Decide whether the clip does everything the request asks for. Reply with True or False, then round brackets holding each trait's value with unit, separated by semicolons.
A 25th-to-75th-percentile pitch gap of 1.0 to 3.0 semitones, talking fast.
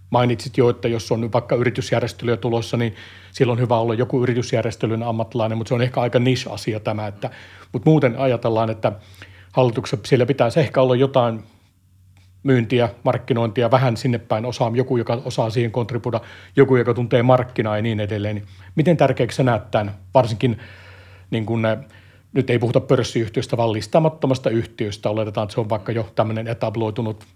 True (2.6 semitones; 165 wpm)